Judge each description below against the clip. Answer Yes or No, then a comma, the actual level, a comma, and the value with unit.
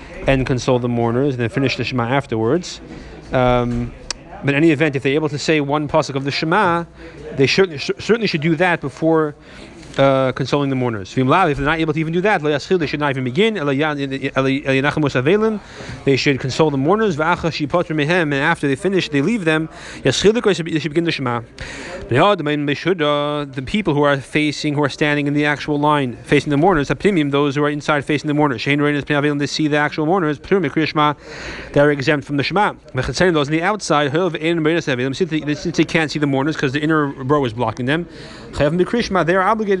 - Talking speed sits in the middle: Yes, average, 180 wpm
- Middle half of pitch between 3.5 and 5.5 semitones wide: No, average, 3.1 semitones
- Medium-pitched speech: Yes, medium, 150 Hz